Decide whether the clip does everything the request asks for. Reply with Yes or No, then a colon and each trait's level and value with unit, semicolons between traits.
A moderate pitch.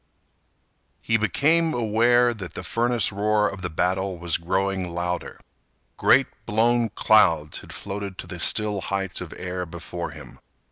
No: low, 100 Hz